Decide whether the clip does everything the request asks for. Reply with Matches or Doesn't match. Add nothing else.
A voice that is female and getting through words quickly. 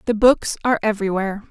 Doesn't match